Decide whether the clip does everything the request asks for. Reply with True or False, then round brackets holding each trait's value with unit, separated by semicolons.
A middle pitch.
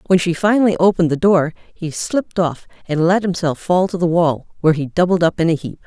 True (175 Hz)